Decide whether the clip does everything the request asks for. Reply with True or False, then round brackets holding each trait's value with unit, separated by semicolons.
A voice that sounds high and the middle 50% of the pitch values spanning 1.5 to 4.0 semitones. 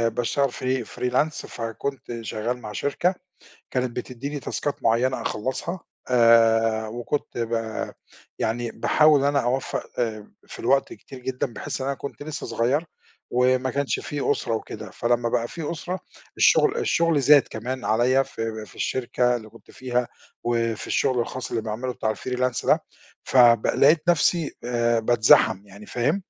False (125 Hz; 3.1 semitones)